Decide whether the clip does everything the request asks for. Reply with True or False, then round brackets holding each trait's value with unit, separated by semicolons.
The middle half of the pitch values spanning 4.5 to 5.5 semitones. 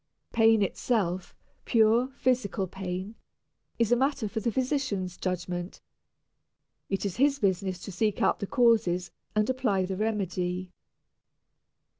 False (4.1 semitones)